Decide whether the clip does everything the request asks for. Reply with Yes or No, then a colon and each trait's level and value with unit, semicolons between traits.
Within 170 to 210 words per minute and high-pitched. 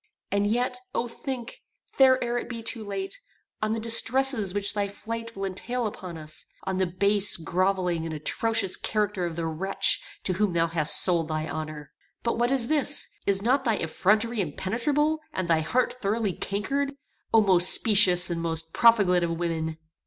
Yes: average, 175 wpm; high, 200 Hz